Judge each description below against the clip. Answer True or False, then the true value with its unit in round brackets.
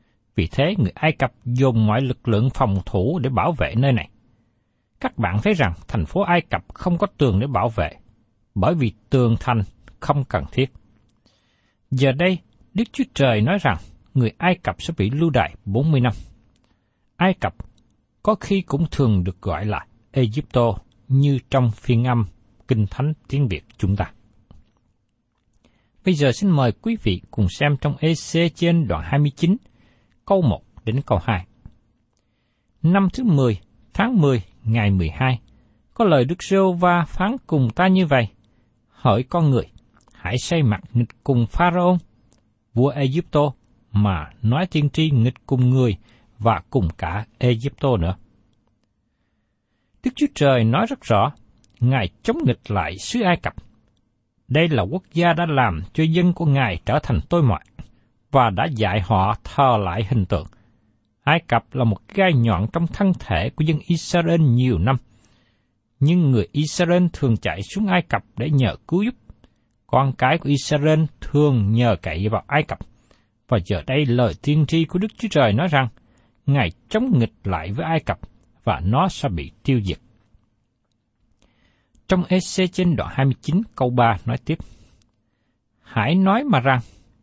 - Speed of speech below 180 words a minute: True (165 wpm)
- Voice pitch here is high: False (120 Hz)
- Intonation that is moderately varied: False (5.7 semitones)